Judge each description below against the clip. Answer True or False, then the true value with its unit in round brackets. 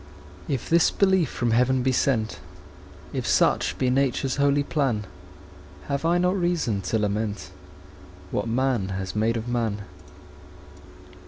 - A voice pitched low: True (125 Hz)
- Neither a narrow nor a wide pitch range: True (4.6 semitones)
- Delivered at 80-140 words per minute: True (135 wpm)